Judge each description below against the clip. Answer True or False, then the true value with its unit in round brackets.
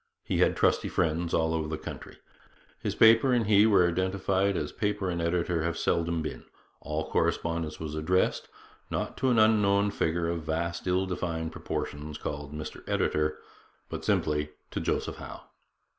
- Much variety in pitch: False (3.5 semitones)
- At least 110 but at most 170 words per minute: True (160 wpm)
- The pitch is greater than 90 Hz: False (85 Hz)